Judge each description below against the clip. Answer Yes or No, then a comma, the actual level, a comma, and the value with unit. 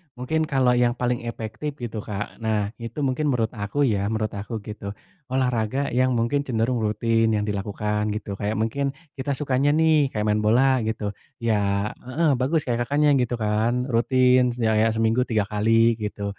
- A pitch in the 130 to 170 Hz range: No, low, 115 Hz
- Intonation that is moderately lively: Yes, average, 3.2 semitones